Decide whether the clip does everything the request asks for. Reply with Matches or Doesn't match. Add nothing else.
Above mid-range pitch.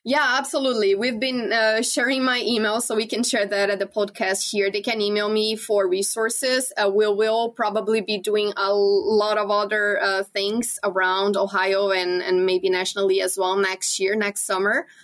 Matches